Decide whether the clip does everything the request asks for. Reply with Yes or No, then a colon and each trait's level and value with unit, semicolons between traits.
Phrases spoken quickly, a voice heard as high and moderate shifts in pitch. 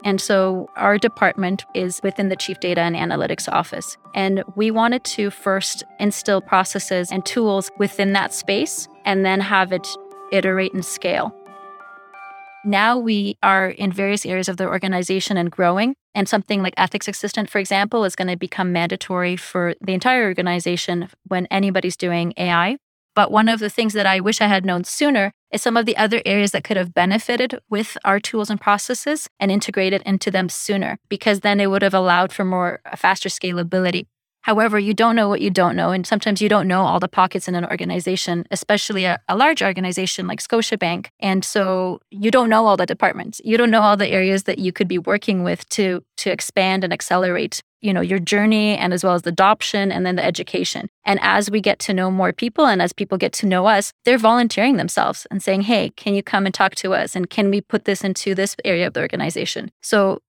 No: fast, 210 wpm; high, 195 Hz; narrow, 2.0 semitones